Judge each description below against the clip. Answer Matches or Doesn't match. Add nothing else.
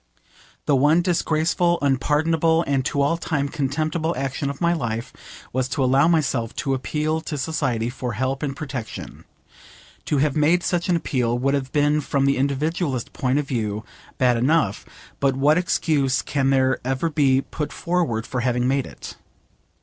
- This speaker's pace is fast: Doesn't match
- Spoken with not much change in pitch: Doesn't match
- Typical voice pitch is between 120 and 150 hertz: Matches